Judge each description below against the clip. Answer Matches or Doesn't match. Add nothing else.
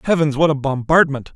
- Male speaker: Matches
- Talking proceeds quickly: Doesn't match